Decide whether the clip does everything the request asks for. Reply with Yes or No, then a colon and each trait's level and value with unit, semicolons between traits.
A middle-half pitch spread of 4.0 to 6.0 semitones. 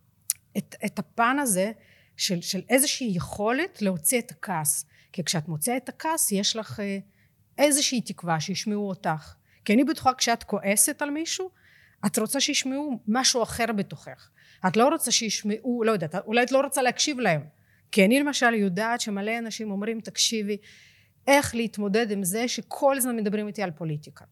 Yes: average, 4.6 semitones